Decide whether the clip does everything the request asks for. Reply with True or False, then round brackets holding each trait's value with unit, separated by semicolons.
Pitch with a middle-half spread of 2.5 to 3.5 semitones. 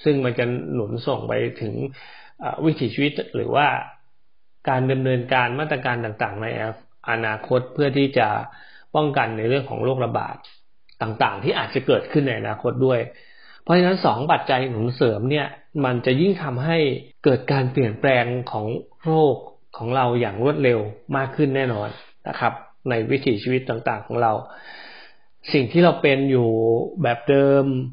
True (2.9 semitones)